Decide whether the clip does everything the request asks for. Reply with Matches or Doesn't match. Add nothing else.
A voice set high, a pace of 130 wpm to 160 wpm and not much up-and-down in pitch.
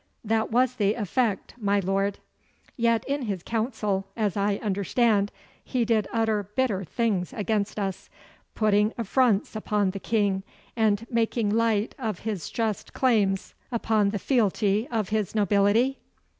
Matches